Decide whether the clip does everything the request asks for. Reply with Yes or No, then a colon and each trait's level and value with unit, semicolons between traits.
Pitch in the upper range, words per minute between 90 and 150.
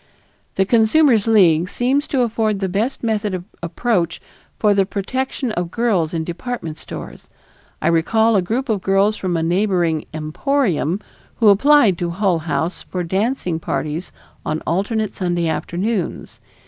Yes: high, 195 Hz; average, 145 wpm